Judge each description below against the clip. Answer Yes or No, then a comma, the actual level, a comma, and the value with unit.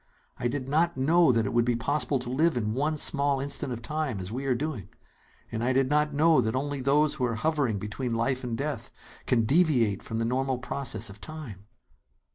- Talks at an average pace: No, fast, 215 wpm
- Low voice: Yes, low, 130 Hz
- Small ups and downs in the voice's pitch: No, average, 4.2 semitones